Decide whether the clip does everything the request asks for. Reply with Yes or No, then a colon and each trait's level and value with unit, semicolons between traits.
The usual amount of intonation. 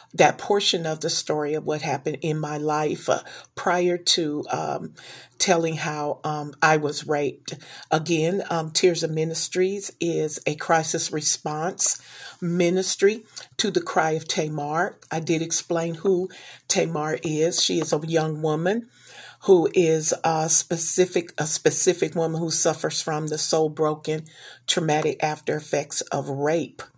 No: narrow, 2.1 semitones